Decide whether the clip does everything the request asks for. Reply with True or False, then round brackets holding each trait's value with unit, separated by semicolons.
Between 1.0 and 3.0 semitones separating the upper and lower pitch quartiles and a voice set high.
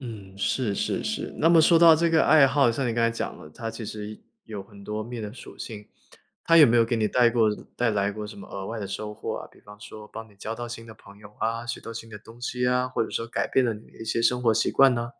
False (2.7 semitones; 115 Hz)